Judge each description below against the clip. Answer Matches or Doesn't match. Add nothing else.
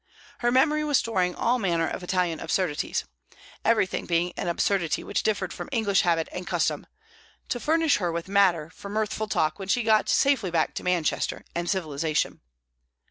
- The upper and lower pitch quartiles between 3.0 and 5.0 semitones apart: Matches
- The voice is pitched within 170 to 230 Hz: Matches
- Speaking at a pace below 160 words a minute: Doesn't match